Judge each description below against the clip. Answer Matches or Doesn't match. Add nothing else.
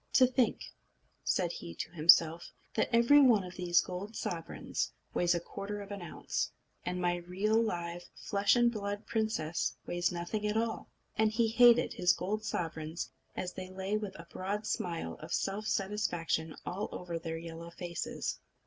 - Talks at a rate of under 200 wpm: Matches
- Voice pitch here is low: Doesn't match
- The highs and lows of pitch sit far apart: Doesn't match